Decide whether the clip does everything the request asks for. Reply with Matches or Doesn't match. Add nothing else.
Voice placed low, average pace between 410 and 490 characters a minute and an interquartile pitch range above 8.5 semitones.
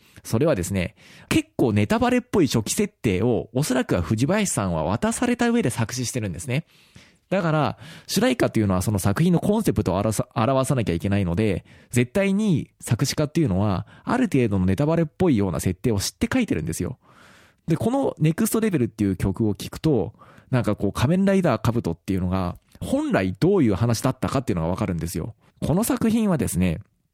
Matches